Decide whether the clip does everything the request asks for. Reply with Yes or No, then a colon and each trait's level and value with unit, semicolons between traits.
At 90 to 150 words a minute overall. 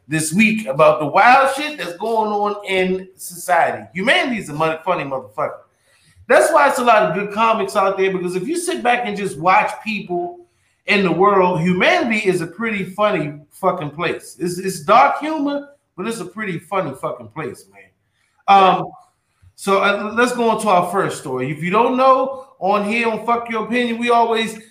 No: average, 190 wpm